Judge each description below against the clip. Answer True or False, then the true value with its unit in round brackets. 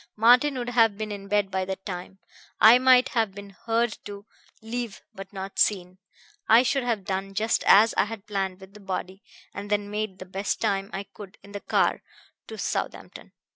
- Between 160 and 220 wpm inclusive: True (195 wpm)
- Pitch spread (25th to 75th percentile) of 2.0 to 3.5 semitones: True (2.7 semitones)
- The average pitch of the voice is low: False (205 Hz)